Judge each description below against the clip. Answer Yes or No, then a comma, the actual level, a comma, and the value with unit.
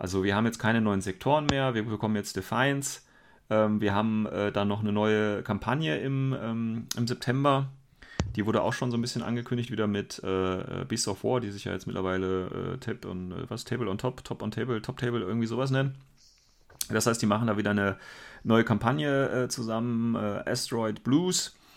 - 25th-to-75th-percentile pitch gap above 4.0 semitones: No, average, 3.4 semitones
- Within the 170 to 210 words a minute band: Yes, average, 185 wpm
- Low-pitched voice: Yes, low, 115 Hz